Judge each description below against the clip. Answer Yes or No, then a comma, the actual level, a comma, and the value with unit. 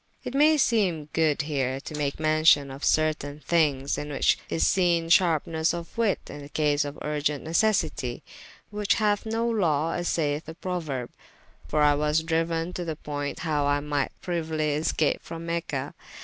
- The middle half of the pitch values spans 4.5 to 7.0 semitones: No, narrow, 2.6 semitones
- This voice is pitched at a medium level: Yes, medium, 155 Hz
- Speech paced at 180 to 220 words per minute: No, average, 170 wpm